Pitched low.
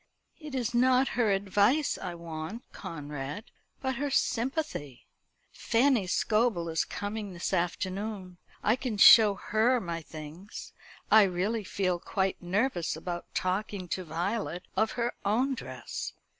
No: high, 200 Hz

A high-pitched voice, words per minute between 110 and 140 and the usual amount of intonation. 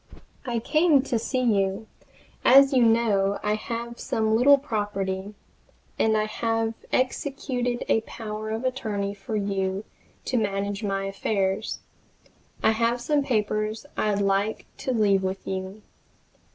Yes: high, 220 Hz; slow, 135 wpm; average, 3.2 semitones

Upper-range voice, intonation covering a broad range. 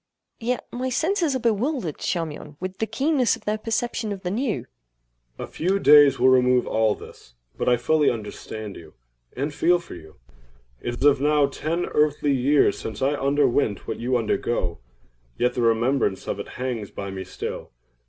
No: medium, 140 Hz; wide, 8.3 semitones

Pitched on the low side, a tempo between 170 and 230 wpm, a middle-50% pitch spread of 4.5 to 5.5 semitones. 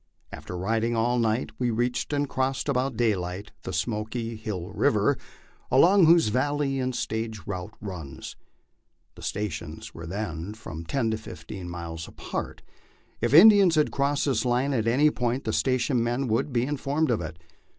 No: low, 115 Hz; average, 160 wpm; average, 5.1 semitones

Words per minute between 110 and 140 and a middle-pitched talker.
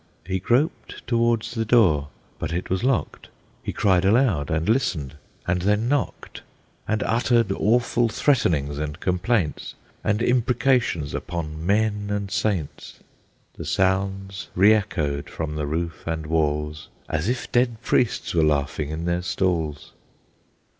No: slow, 135 wpm; very low, 95 Hz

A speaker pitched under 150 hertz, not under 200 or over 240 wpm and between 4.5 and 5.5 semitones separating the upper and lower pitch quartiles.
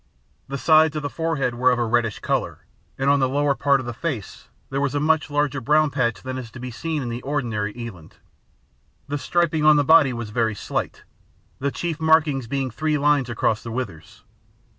No: low, 135 Hz; fast, 205 wpm; average, 3.8 semitones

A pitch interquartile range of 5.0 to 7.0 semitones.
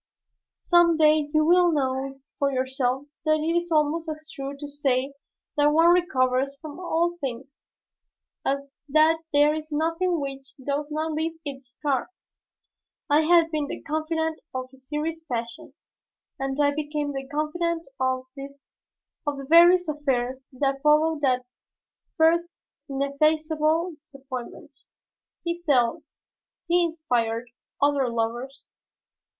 No: average, 3.0 semitones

